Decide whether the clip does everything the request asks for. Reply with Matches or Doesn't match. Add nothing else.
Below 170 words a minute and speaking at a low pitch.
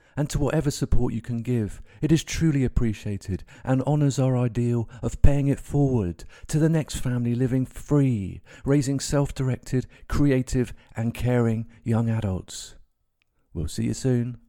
Matches